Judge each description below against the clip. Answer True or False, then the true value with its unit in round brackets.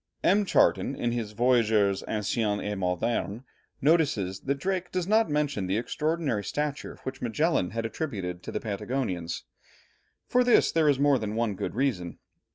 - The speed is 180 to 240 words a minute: False (160 wpm)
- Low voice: True (120 Hz)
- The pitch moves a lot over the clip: True (6.5 semitones)